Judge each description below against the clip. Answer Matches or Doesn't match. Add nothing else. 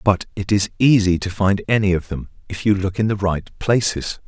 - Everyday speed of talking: Doesn't match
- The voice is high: Doesn't match